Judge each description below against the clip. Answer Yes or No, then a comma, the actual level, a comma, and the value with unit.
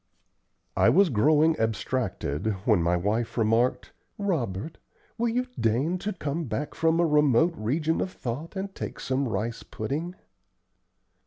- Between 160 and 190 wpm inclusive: No, average, 140 wpm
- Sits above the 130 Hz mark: Yes, medium, 140 Hz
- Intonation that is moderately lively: No, wide, 6.7 semitones